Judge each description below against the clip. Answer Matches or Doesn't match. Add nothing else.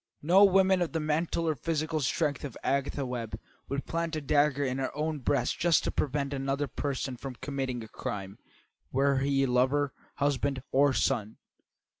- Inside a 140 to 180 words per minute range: Matches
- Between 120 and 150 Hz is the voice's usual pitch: Matches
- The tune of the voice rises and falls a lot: Doesn't match